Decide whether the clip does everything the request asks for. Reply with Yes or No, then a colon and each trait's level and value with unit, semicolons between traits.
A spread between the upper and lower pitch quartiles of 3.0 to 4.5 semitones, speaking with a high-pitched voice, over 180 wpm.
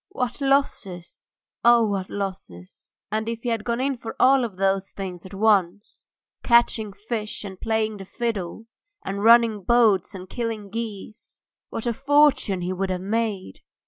No: average, 3.4 semitones; high, 215 Hz; average, 155 wpm